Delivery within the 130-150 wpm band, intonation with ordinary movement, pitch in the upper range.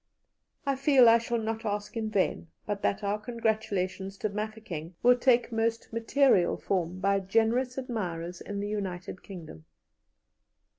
Yes: average, 145 wpm; average, 3.2 semitones; high, 215 Hz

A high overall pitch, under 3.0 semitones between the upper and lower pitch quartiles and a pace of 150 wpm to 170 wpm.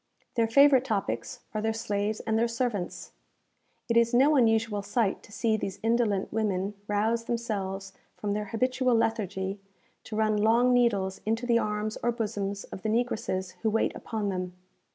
Yes: high, 220 Hz; narrow, 2.5 semitones; average, 165 wpm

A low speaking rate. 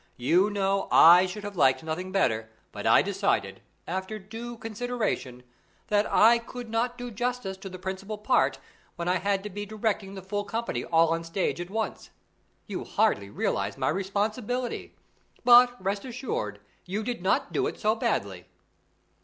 No: average, 165 wpm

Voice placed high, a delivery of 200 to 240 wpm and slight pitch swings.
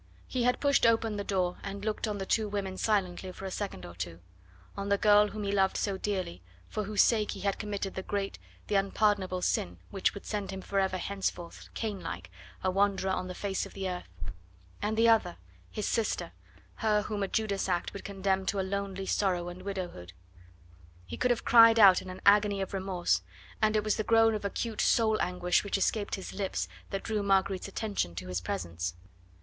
Yes: high, 195 Hz; fast, 205 wpm; narrow, 2.0 semitones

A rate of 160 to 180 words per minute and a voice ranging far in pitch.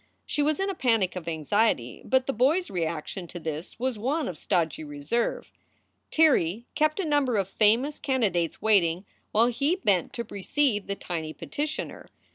Yes: average, 170 wpm; wide, 8.2 semitones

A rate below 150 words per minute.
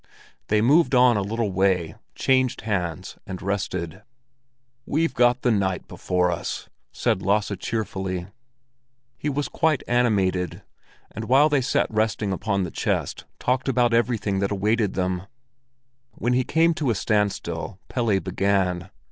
Yes: average, 140 wpm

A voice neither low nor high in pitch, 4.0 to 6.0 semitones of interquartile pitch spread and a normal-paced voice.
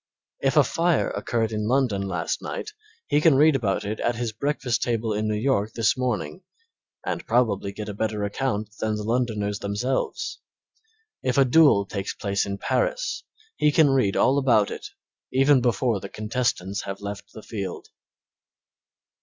No: low, 110 Hz; average, 4.4 semitones; average, 165 wpm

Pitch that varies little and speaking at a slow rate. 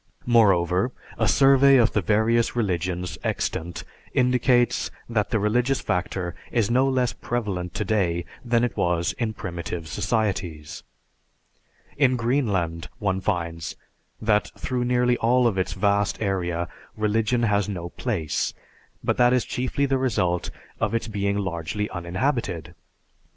No: average, 5.3 semitones; slow, 130 wpm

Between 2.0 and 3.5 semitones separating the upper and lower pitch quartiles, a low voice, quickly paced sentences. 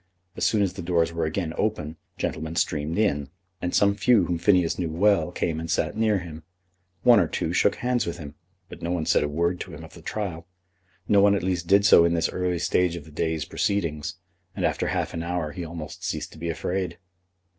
Yes: average, 3.2 semitones; very low, 85 Hz; fast, 225 wpm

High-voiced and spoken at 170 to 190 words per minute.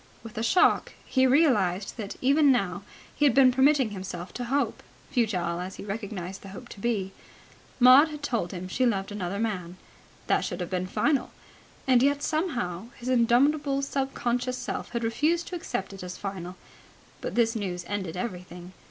Yes: high, 225 Hz; average, 180 wpm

